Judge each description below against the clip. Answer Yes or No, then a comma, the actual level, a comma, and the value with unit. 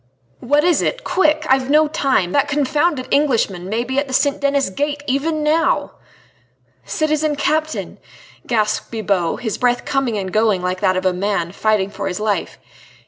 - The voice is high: Yes, very high, 255 Hz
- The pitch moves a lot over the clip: Yes, wide, 6.5 semitones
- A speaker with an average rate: Yes, average, 170 wpm